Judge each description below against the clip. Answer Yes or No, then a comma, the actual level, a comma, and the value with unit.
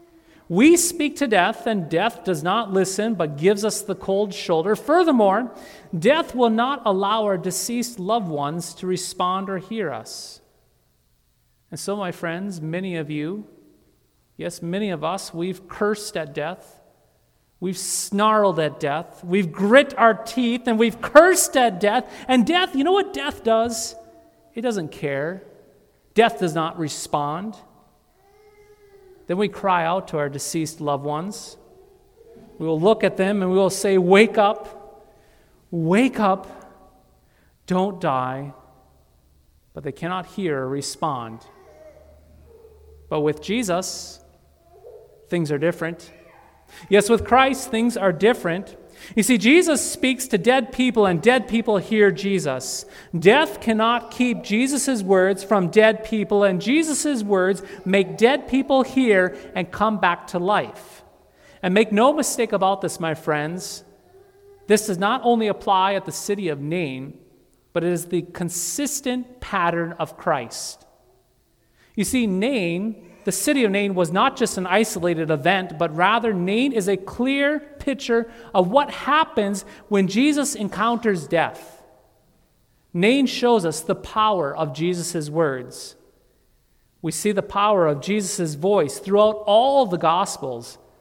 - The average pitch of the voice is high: Yes, high, 200 Hz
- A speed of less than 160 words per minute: Yes, average, 145 wpm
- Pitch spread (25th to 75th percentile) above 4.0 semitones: Yes, wide, 5.4 semitones